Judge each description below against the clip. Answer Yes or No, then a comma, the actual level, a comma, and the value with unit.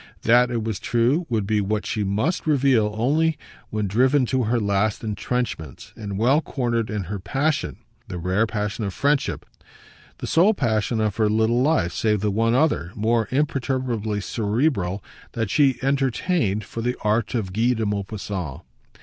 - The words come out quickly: No, average, 165 wpm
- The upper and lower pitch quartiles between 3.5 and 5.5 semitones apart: Yes, average, 3.9 semitones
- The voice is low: Yes, low, 115 Hz